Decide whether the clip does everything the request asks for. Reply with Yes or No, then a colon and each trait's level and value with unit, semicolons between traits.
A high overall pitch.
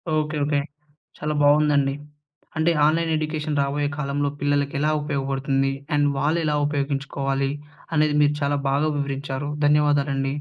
No: medium, 145 Hz